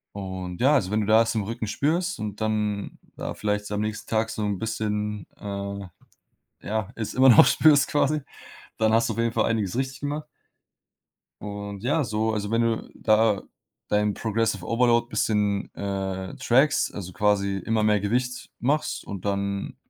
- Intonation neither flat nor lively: No, narrow, 2.3 semitones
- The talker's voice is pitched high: No, low, 110 Hz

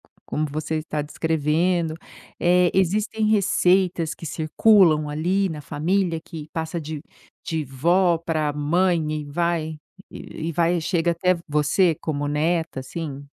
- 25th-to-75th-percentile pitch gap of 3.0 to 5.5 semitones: No, narrow, 2.6 semitones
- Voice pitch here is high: No, medium, 165 Hz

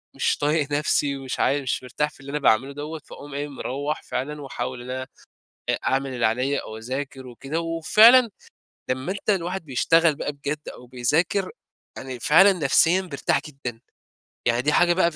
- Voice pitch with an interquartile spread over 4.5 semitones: No, average, 3.8 semitones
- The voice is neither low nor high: Yes, medium, 145 Hz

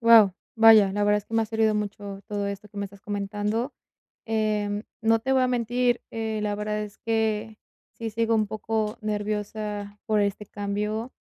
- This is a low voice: No, high, 215 Hz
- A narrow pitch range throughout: Yes, narrow, 1.5 semitones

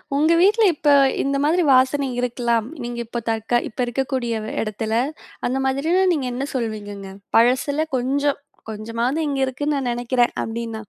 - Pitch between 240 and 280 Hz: Yes, very high, 250 Hz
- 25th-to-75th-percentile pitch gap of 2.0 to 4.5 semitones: Yes, average, 3.4 semitones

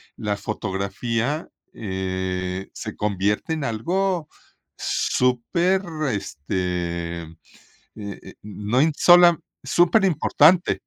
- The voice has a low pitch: Yes, low, 110 Hz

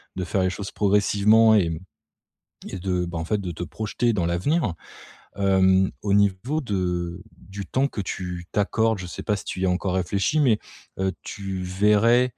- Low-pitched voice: Yes, very low, 95 Hz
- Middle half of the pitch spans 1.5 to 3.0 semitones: Yes, average, 2.7 semitones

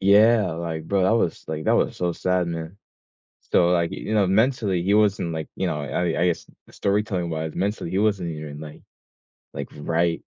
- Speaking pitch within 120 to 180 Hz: No, very low, 90 Hz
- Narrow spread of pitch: No, average, 3.5 semitones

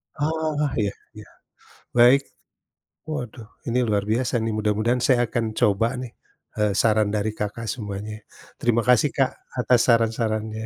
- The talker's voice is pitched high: No, low, 115 Hz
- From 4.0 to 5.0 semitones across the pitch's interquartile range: No, average, 2.7 semitones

